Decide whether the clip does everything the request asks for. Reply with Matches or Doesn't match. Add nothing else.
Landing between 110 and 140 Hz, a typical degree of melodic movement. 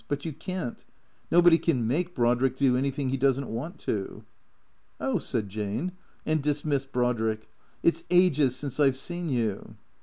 Matches